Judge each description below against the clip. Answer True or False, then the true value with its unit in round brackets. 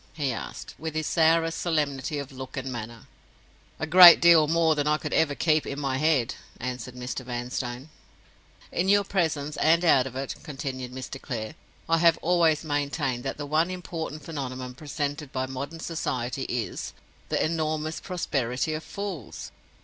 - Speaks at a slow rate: False (160 wpm)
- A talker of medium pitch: True (145 Hz)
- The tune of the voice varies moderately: True (3.8 semitones)